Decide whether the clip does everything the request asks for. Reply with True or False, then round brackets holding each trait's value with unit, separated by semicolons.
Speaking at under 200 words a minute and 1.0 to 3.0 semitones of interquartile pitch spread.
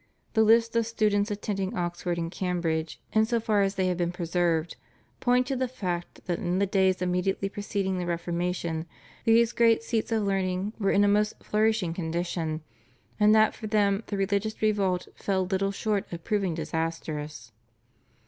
False (170 wpm; 3.6 semitones)